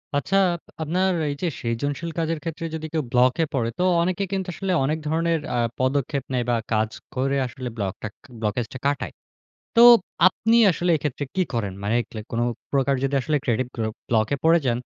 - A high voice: No, medium, 140 Hz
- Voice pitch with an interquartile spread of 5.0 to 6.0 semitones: Yes, wide, 5.5 semitones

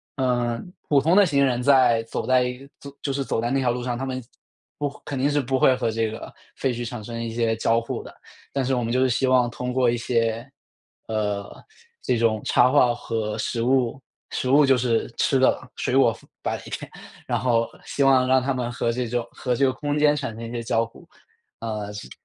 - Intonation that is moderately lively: No, narrow, 2.3 semitones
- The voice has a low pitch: Yes, low, 125 Hz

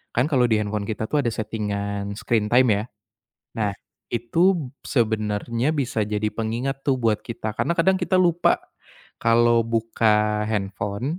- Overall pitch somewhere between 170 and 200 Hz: No, low, 115 Hz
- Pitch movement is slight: No, average, 3.8 semitones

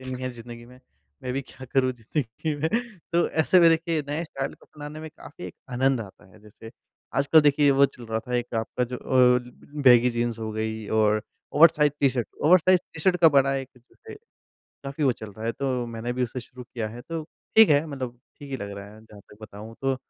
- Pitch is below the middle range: Yes, low, 130 Hz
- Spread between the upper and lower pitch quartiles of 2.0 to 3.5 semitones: No, average, 4.1 semitones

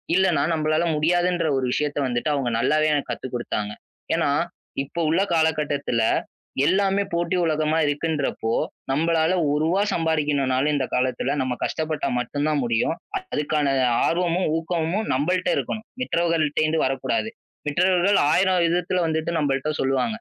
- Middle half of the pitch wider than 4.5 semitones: No, average, 3.3 semitones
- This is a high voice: No, medium, 155 Hz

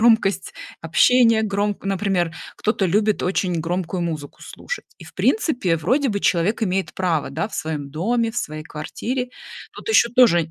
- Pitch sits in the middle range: No, high, 195 Hz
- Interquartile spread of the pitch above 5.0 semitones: Yes, wide, 5.4 semitones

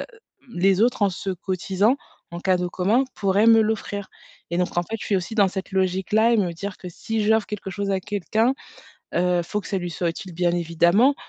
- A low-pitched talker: No, high, 190 Hz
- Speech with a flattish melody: No, average, 3.1 semitones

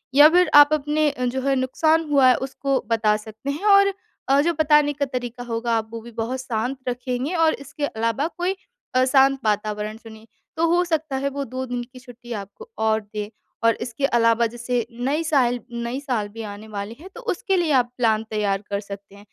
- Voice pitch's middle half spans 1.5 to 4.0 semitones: No, average, 4.5 semitones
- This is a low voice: No, very high, 250 Hz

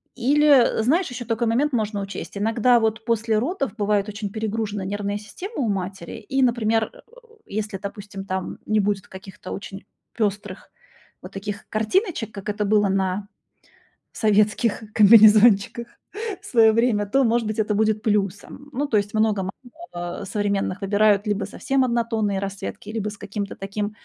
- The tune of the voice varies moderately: No, narrow, 2.2 semitones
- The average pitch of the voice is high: Yes, high, 215 Hz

